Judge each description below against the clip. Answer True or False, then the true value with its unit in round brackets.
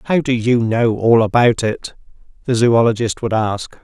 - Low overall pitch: True (115 Hz)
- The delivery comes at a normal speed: True (170 wpm)